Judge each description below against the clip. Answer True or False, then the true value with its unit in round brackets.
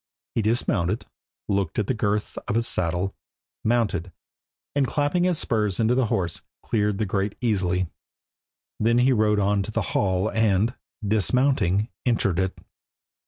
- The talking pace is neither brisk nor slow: True (145 wpm)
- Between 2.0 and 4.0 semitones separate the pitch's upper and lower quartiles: True (3.3 semitones)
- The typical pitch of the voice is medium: False (105 Hz)